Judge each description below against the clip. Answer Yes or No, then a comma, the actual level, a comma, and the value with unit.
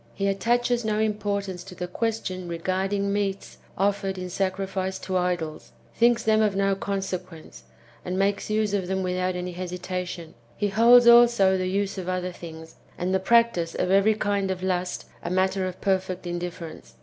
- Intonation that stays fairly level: Yes, narrow, 1.9 semitones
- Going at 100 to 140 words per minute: No, average, 170 wpm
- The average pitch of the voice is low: No, high, 190 Hz